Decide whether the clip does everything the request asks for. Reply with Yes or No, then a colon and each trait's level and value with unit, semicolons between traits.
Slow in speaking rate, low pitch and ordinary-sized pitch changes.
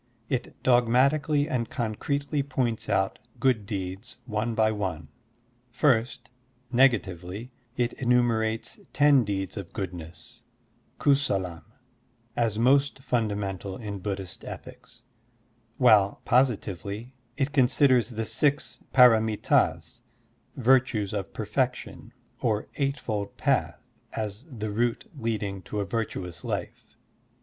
Yes: slow, 105 wpm; low, 115 Hz; average, 4.1 semitones